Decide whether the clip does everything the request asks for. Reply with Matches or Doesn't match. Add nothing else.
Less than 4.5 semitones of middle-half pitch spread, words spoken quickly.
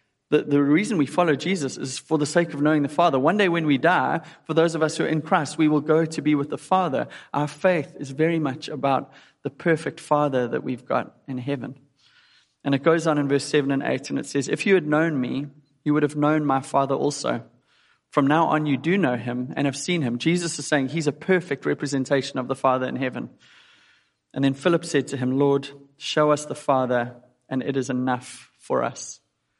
Matches